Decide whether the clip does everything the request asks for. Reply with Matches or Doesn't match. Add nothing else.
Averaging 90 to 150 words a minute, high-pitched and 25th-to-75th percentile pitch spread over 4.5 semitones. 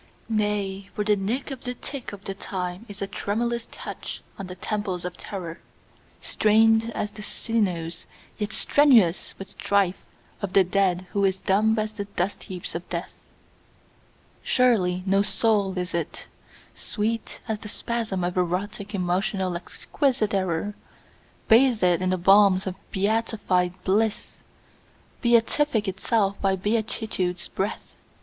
Doesn't match